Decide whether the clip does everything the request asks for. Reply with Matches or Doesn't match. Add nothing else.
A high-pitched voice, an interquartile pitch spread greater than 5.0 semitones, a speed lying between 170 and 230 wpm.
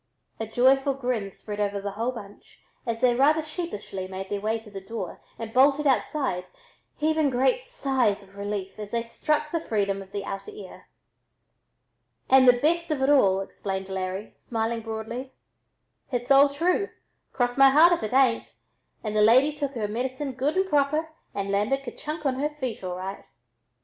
Matches